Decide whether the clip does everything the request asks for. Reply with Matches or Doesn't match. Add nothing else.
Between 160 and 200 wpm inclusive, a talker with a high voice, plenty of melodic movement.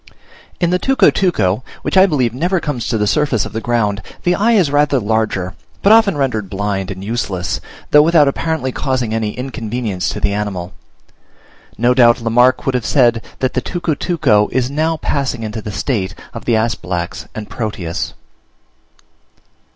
Doesn't match